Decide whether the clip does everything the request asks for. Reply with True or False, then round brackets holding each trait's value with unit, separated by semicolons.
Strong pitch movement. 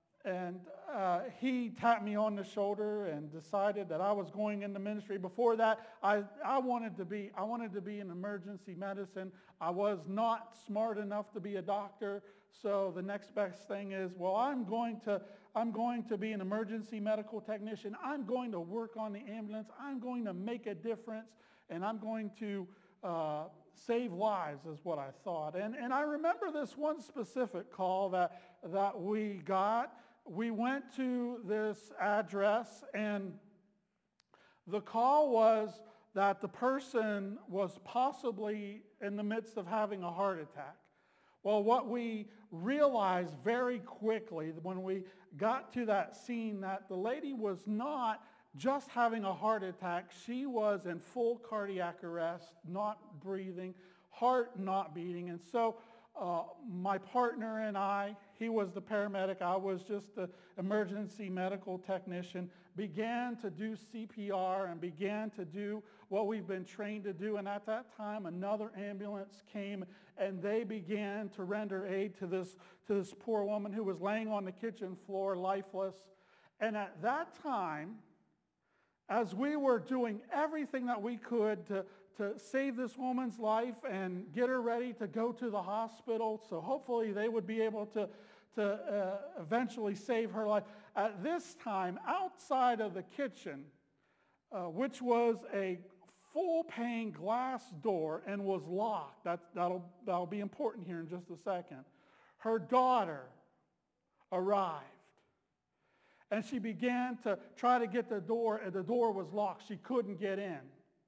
False (2.9 semitones)